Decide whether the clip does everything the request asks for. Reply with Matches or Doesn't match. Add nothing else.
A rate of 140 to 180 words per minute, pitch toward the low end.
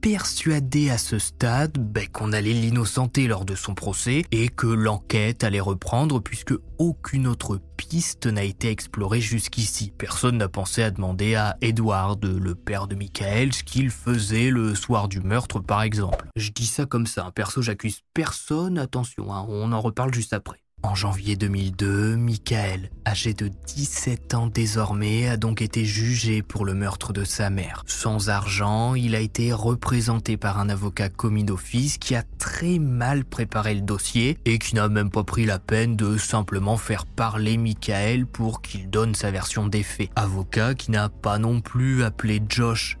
Matches